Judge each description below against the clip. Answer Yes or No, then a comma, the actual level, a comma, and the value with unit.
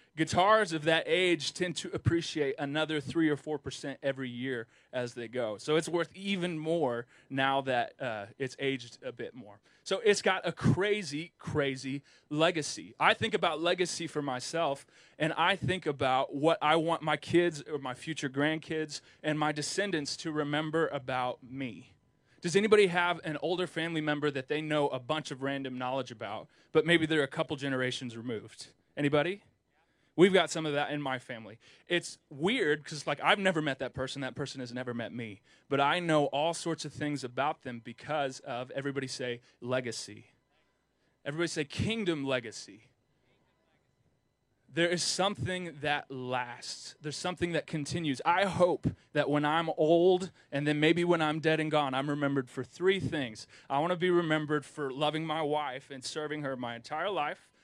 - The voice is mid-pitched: Yes, medium, 150 Hz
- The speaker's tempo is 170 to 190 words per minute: Yes, average, 180 wpm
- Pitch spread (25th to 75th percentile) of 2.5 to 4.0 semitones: Yes, average, 3.7 semitones